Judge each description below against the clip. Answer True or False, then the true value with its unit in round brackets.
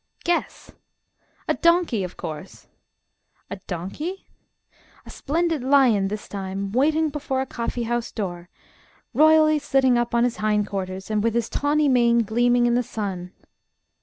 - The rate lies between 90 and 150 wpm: True (140 wpm)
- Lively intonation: True (6.0 semitones)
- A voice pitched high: True (240 Hz)